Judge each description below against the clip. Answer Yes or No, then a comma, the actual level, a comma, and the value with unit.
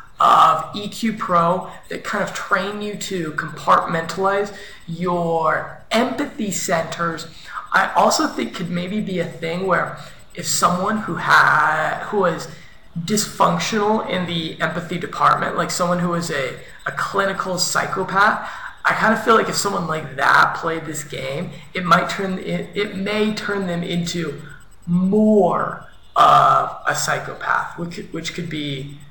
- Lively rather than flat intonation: No, average, 3.3 semitones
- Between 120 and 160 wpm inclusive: Yes, average, 145 wpm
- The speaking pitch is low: No, medium, 175 Hz